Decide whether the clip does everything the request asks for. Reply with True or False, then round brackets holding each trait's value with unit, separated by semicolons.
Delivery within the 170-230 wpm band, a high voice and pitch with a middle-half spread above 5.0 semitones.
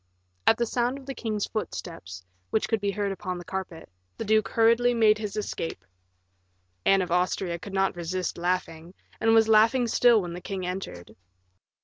False (175 wpm; 195 Hz; 4.0 semitones)